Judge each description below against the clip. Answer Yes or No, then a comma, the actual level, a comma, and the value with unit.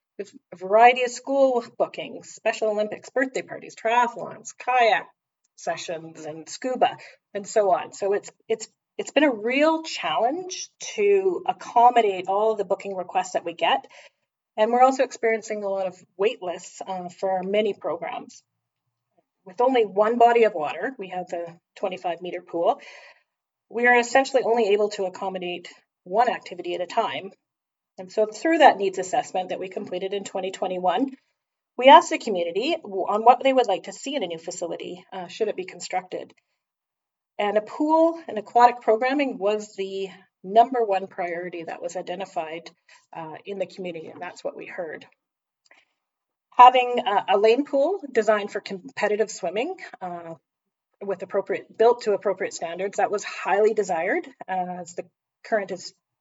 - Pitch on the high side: Yes, high, 210 Hz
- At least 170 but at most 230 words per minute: No, average, 160 wpm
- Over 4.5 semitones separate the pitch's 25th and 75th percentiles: Yes, average, 4.9 semitones